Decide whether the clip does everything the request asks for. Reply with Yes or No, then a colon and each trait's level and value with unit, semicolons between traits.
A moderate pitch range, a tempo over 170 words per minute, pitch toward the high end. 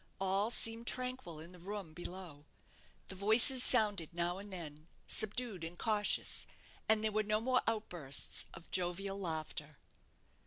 No: average, 4.1 semitones; average, 145 wpm; high, 195 Hz